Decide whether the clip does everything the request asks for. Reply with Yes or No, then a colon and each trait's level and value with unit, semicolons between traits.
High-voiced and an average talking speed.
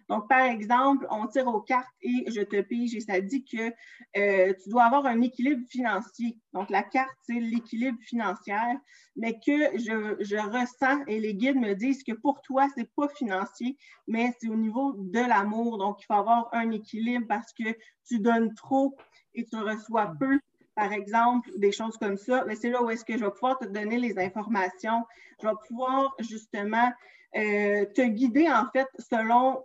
Yes: high, 235 Hz; average, 190 wpm